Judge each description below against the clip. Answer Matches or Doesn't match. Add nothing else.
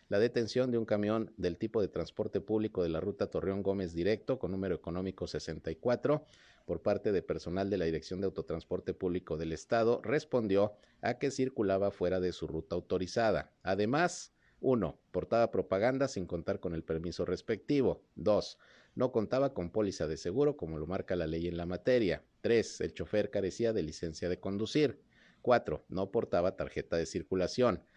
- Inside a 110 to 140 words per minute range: Doesn't match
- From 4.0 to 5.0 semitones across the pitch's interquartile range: Matches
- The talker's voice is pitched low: Matches